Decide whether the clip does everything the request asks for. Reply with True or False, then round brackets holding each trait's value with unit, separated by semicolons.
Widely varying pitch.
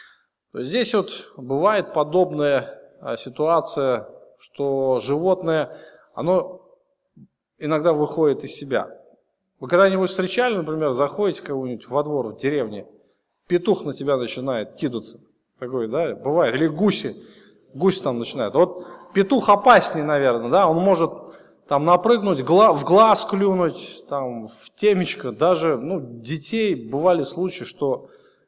True (5.8 semitones)